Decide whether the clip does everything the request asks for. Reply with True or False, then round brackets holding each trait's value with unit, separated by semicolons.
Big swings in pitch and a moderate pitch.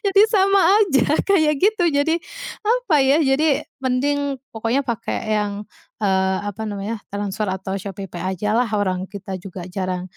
False (6.9 semitones; 220 Hz)